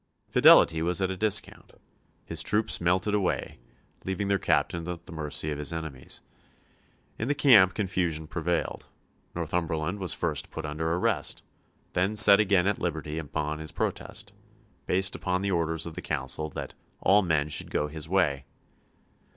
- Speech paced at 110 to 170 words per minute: Yes, average, 160 wpm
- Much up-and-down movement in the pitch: No, average, 3.5 semitones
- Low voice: Yes, very low, 85 Hz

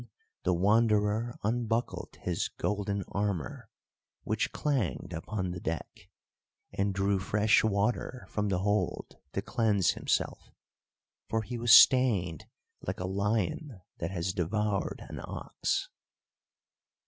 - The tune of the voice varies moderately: Yes, average, 3.1 semitones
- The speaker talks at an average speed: No, slow, 120 wpm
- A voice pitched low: Yes, low, 105 Hz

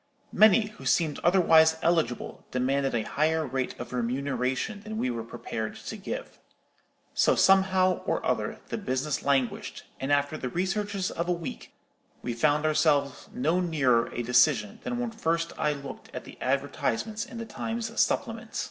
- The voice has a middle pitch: Yes, medium, 155 Hz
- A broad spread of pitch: Yes, wide, 6.4 semitones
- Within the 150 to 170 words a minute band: Yes, average, 160 wpm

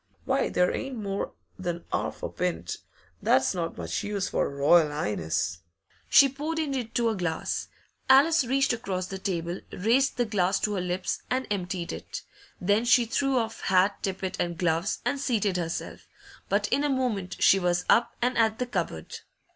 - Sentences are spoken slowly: No, average, 180 wpm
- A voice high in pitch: Yes, high, 195 Hz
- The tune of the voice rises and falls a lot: Yes, wide, 5.7 semitones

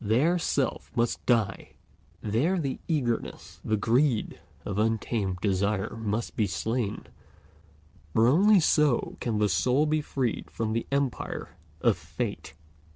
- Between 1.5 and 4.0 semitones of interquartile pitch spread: No, average, 4.8 semitones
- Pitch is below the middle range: Yes, low, 115 Hz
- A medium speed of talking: No, slow, 130 wpm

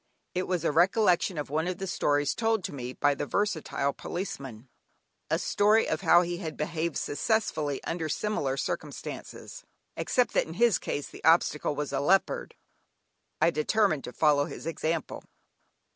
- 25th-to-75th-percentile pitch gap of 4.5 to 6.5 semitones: Yes, average, 4.9 semitones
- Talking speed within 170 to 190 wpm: No, average, 160 wpm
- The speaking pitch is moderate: Yes, medium, 165 Hz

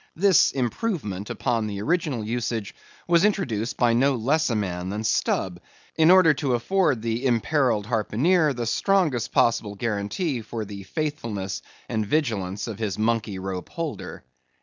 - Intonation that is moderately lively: No, wide, 6.3 semitones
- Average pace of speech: Yes, average, 150 wpm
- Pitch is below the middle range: Yes, low, 115 Hz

